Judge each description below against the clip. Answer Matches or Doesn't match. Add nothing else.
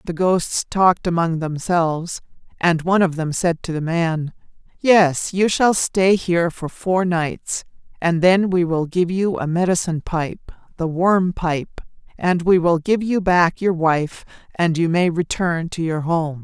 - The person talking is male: Doesn't match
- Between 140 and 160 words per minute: Doesn't match